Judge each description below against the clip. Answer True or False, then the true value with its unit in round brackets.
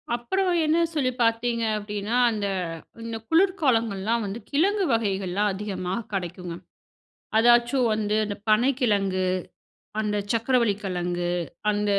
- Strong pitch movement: False (3.4 semitones)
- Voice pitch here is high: True (215 Hz)